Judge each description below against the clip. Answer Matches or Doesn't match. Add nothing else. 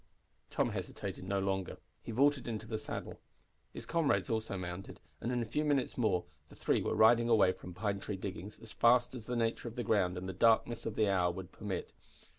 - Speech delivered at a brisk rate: Matches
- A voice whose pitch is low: Matches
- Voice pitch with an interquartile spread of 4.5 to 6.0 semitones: Doesn't match